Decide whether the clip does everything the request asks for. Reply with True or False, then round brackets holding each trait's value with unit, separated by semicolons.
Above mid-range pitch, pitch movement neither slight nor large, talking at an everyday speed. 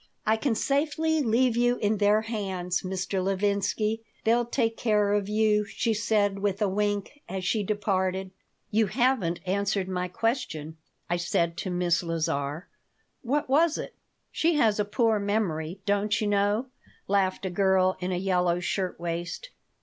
True (205 Hz; 3.2 semitones; 155 wpm)